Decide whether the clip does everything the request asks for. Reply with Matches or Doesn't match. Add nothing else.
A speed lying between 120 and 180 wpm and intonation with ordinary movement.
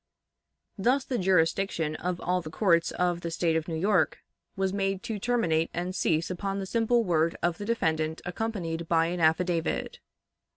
Matches